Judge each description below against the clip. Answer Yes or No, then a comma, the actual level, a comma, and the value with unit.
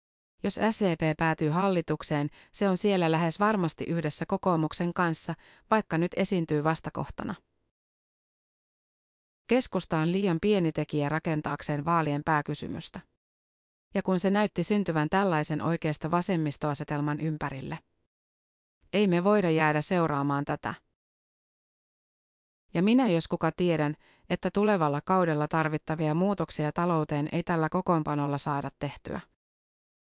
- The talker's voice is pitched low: No, medium, 160 Hz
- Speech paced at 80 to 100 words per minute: No, average, 110 wpm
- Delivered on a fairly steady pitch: No, average, 3.7 semitones